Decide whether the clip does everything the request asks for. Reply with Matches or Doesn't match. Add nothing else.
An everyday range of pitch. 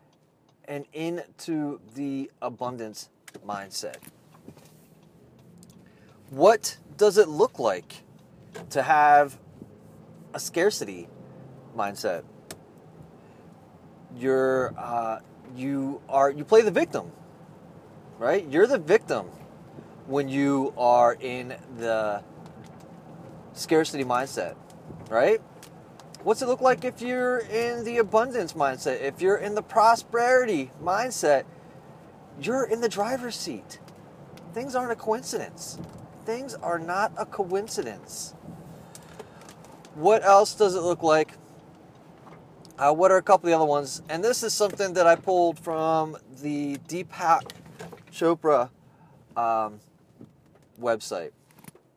Doesn't match